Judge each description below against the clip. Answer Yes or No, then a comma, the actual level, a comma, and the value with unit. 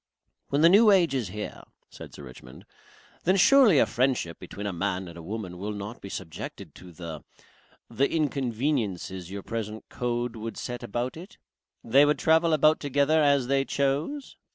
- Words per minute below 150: No, average, 175 wpm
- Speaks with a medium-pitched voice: No, low, 120 Hz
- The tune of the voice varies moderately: No, wide, 7.0 semitones